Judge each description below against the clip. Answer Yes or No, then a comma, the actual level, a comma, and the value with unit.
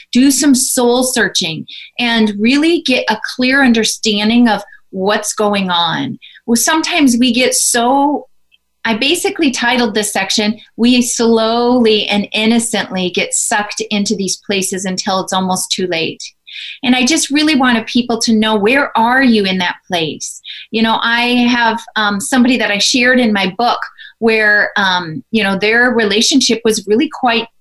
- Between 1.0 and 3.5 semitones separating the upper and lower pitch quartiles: Yes, average, 3.1 semitones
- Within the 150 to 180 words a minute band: Yes, average, 160 wpm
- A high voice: Yes, high, 230 Hz